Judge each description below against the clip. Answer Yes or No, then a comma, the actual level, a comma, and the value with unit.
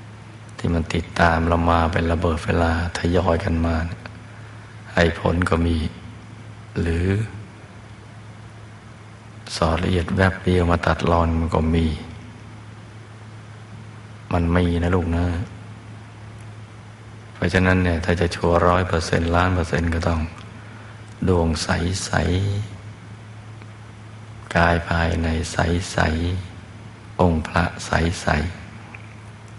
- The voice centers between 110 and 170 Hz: No, very low, 95 Hz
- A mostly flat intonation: No, average, 4.3 semitones